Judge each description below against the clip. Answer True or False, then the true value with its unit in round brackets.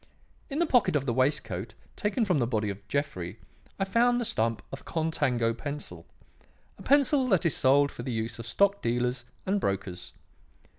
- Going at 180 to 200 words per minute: True (185 wpm)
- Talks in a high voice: False (135 Hz)